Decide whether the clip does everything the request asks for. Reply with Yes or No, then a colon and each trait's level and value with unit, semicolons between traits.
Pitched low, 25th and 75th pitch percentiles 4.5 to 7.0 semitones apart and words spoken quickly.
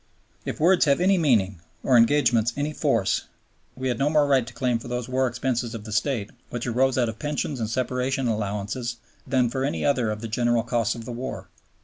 No: low, 125 Hz; average, 2.8 semitones; fast, 215 wpm